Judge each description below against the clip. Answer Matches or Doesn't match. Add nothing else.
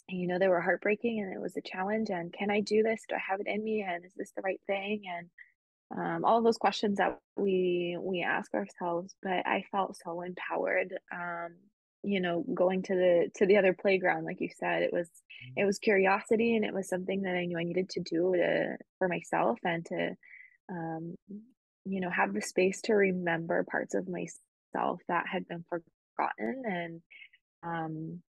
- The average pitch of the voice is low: Doesn't match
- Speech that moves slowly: Doesn't match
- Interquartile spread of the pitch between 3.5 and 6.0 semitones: Doesn't match